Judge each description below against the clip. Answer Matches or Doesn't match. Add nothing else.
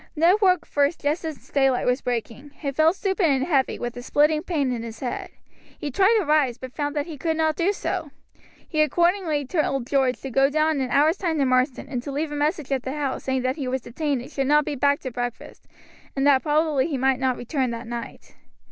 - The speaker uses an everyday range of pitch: Matches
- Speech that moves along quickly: Matches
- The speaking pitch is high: Matches